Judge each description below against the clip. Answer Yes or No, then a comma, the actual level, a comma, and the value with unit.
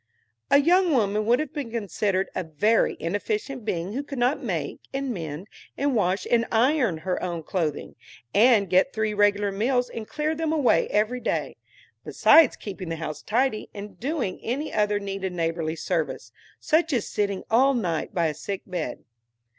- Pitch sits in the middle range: No, high, 210 Hz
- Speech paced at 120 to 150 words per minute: No, average, 170 wpm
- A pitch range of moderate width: No, wide, 6.0 semitones